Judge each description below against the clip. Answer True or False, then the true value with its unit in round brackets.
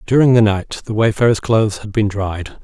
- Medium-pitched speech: False (110 Hz)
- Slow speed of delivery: False (205 wpm)